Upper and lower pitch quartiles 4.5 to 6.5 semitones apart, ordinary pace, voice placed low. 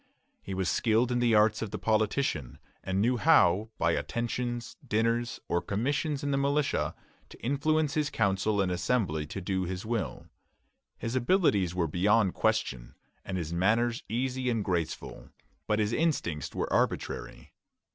Yes: average, 4.8 semitones; average, 155 wpm; low, 110 Hz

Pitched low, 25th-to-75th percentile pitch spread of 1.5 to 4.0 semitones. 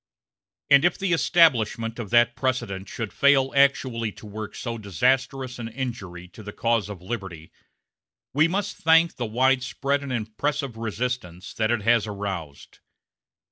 No: low, 120 Hz; average, 4.4 semitones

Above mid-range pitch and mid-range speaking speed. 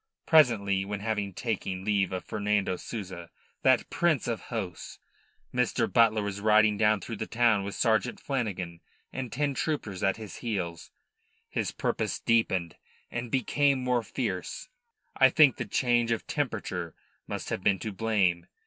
No: low, 110 Hz; average, 150 wpm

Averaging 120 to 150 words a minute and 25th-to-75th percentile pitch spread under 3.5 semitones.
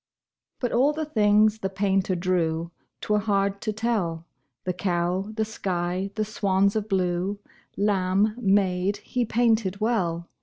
Yes: average, 140 wpm; average, 2.8 semitones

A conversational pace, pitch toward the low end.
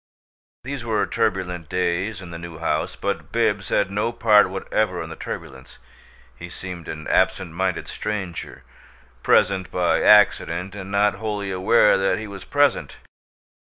Yes: average, 150 wpm; very low, 95 Hz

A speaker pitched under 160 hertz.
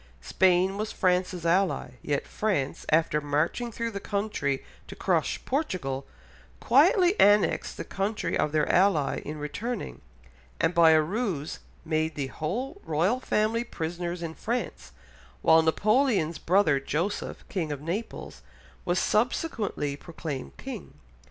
No: medium, 180 Hz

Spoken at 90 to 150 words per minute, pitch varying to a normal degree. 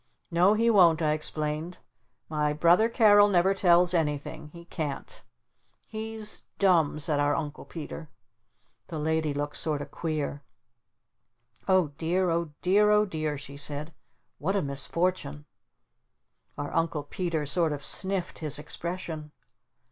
Yes: slow, 135 wpm; average, 3.5 semitones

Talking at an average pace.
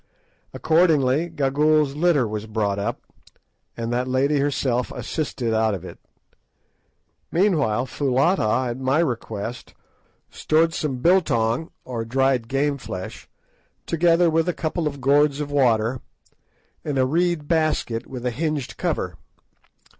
No: slow, 125 wpm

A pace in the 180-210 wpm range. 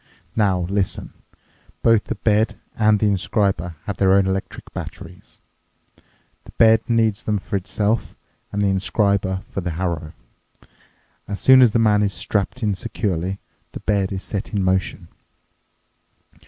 No: average, 145 wpm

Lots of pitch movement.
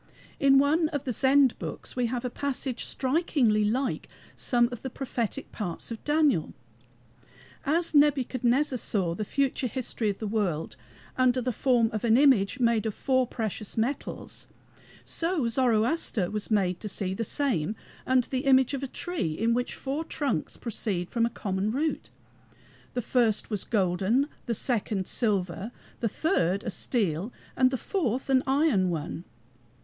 No: average, 4.4 semitones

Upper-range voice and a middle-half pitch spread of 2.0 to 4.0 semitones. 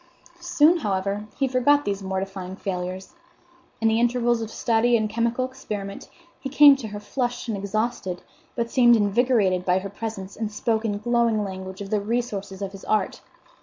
Yes: high, 215 Hz; average, 3.6 semitones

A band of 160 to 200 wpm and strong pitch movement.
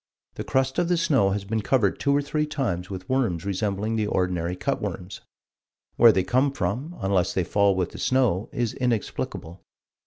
Yes: average, 185 wpm; wide, 6.0 semitones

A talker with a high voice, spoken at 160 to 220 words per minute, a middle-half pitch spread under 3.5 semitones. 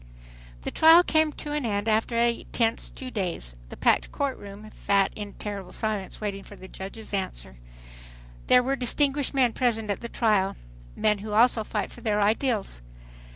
No: high, 215 Hz; average, 170 wpm; average, 3.9 semitones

